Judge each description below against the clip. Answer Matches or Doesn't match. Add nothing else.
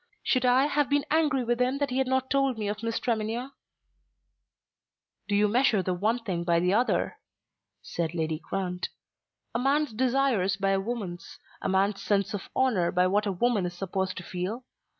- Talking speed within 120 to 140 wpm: Doesn't match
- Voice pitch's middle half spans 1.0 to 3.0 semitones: Doesn't match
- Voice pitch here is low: Doesn't match